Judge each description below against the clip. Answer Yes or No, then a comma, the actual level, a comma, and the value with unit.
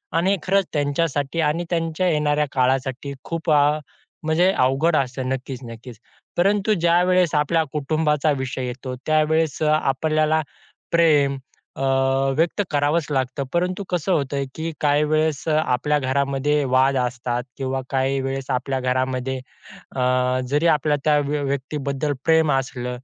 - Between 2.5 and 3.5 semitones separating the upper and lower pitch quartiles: Yes, average, 3.1 semitones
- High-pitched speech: No, medium, 145 Hz